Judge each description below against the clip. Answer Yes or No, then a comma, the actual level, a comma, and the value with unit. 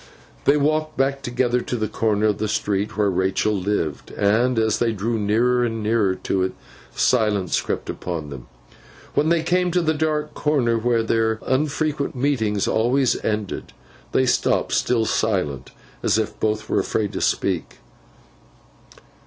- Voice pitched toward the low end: Yes, low, 115 Hz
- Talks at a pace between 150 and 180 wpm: Yes, average, 155 wpm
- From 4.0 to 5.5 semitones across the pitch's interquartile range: Yes, average, 4.3 semitones